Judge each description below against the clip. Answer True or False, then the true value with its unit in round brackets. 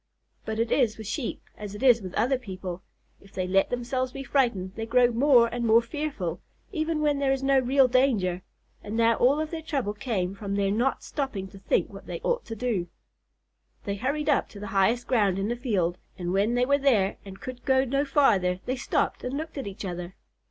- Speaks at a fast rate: True (220 wpm)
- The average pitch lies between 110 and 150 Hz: False (235 Hz)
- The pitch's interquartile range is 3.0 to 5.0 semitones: False (5.4 semitones)